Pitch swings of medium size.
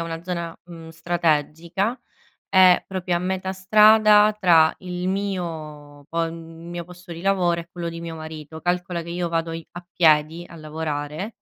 No: narrow, 2.0 semitones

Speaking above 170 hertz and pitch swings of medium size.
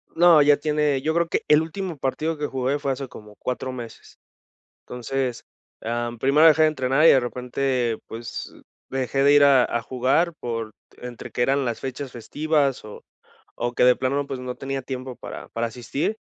No: low, 135 Hz; average, 3.1 semitones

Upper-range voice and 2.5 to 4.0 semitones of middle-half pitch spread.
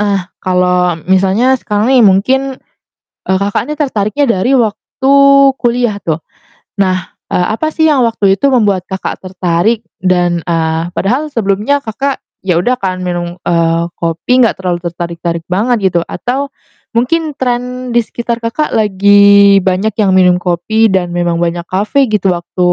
No: high, 200 Hz; average, 5.1 semitones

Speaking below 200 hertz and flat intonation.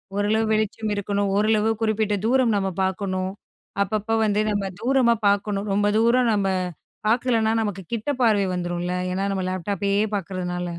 No: high, 205 Hz; narrow, 2.2 semitones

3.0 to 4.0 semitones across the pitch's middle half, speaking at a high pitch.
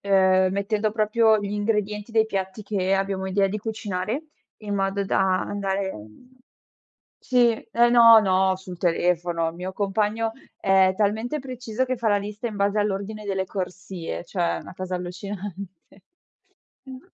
No: narrow, 2.6 semitones; high, 200 Hz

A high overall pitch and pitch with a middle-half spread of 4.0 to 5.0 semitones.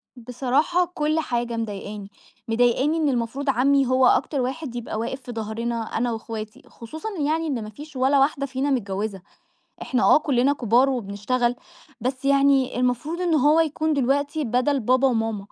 No: very high, 255 Hz; average, 3.6 semitones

